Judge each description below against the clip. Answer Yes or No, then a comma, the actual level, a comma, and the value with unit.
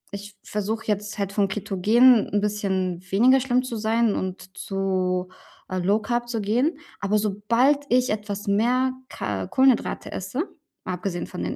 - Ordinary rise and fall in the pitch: Yes, average, 3.6 semitones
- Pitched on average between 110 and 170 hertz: No, high, 210 Hz